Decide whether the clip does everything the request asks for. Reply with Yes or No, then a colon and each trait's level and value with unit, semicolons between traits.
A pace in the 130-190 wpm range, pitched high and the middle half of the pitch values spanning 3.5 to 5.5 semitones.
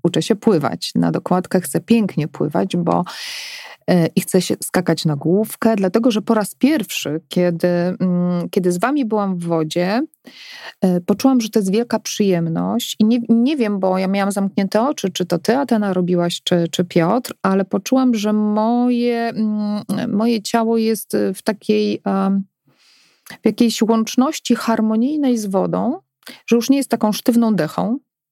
Yes: average, 155 wpm; high, 210 Hz; average, 4.2 semitones